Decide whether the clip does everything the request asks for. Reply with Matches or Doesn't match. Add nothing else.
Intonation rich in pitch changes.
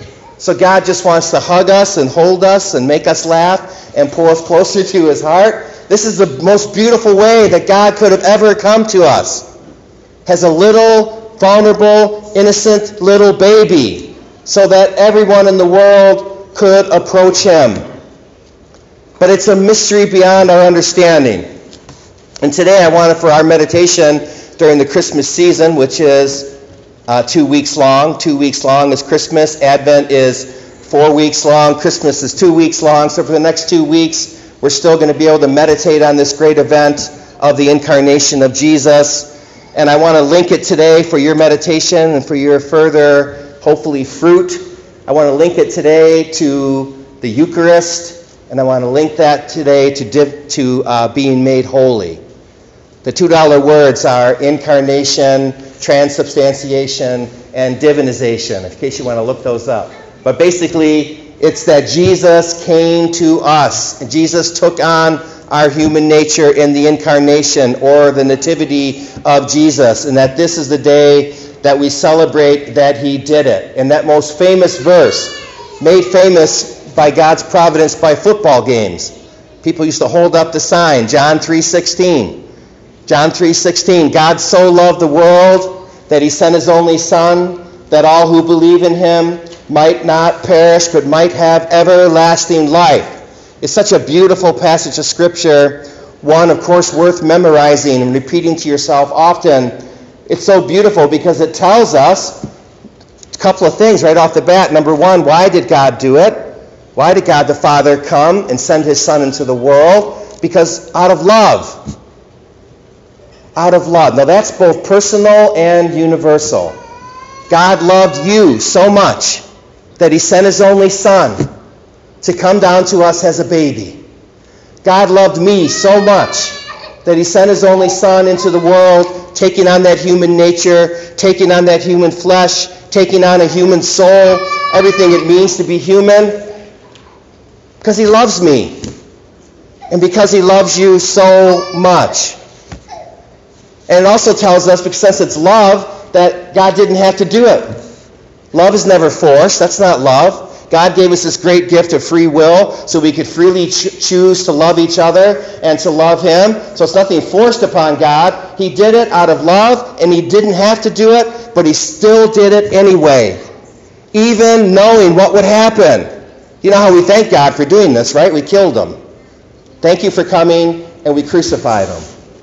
Doesn't match